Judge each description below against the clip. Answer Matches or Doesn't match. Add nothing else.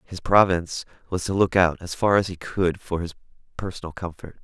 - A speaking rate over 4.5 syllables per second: Matches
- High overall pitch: Doesn't match